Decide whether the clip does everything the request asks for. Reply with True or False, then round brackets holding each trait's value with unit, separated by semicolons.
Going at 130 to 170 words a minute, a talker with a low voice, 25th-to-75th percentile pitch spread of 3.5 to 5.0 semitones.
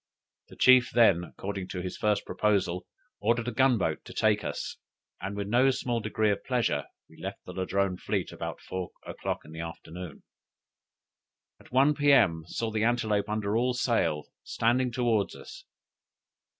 True (165 wpm; 105 Hz; 4.6 semitones)